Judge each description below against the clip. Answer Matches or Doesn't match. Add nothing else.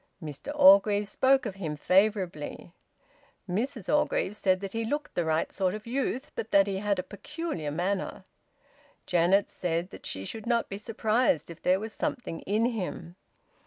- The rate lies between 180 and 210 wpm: Doesn't match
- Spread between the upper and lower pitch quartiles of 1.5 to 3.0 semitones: Doesn't match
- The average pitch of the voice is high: Matches